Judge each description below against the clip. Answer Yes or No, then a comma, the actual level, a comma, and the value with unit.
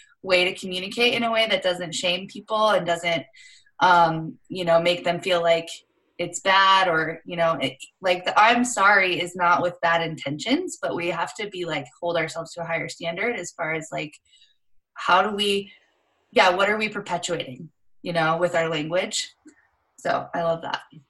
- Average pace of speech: Yes, average, 190 wpm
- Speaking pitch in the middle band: Yes, medium, 175 Hz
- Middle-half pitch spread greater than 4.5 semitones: No, average, 3.4 semitones